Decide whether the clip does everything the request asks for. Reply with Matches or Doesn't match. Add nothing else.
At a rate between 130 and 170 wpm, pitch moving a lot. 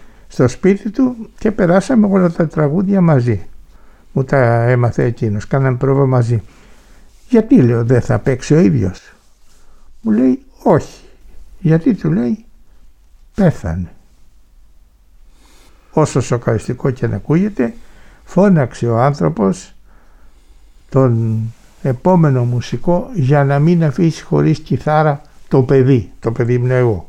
Doesn't match